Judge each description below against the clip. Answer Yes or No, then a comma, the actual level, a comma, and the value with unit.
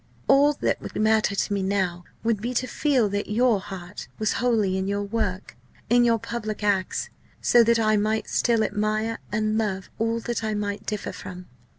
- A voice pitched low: No, high, 215 Hz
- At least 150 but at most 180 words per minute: No, average, 190 wpm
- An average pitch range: No, narrow, 2.2 semitones